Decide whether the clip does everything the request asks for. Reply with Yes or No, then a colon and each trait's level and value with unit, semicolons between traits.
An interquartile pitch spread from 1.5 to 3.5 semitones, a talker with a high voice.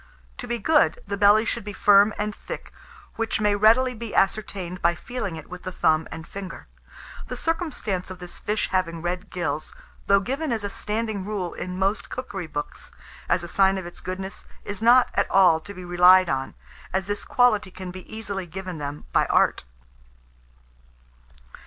Yes: average, 3.2 semitones; high, 195 Hz